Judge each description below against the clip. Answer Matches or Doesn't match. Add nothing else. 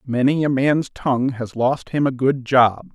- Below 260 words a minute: Matches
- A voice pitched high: Doesn't match